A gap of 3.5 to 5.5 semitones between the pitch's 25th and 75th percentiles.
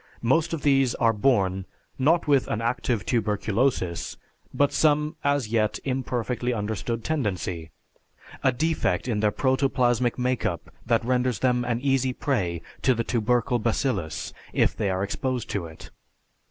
Yes: average, 4.0 semitones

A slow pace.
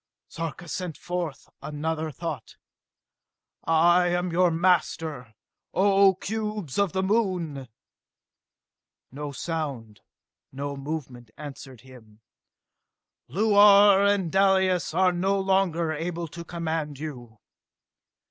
Yes: slow, 100 wpm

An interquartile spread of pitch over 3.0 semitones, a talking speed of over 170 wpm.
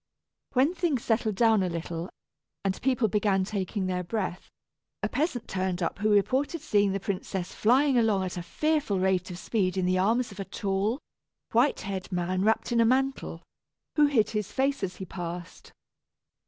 Yes: average, 4.6 semitones; average, 180 wpm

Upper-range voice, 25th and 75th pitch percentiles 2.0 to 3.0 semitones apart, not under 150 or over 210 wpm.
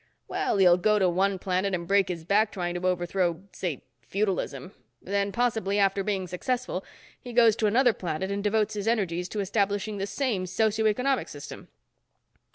Yes: high, 200 Hz; average, 2.7 semitones; average, 170 wpm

